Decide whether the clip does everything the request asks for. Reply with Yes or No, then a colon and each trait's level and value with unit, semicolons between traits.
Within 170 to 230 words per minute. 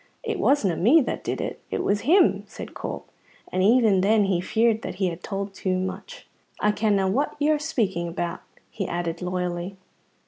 Yes: average, 180 wpm